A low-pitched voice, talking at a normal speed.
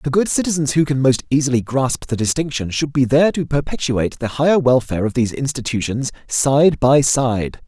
Yes: low, 130 Hz; average, 190 wpm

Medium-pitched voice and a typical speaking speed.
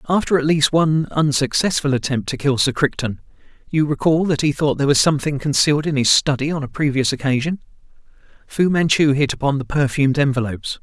Yes: medium, 145 Hz; average, 170 wpm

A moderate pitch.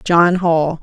Yes: medium, 170 Hz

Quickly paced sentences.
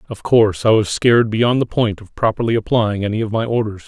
Yes: fast, 230 wpm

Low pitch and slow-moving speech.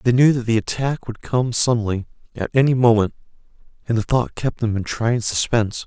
No: low, 120 Hz; average, 195 wpm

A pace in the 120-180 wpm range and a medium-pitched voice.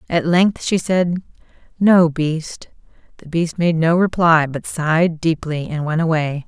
Yes: average, 160 wpm; medium, 165 Hz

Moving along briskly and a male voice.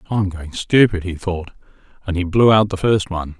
Yes: fast, 210 wpm; male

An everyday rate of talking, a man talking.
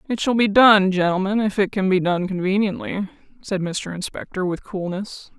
No: average, 180 wpm; female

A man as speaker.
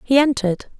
No: female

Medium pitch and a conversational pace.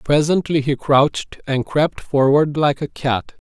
Yes: medium, 145 Hz; average, 155 wpm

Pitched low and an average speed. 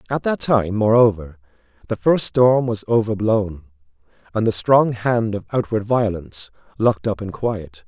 Yes: low, 105 Hz; average, 150 wpm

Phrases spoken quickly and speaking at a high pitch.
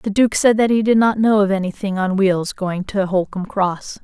Yes: fast, 240 wpm; high, 200 Hz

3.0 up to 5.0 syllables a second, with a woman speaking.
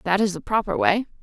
No: 6.1 syllables/s; female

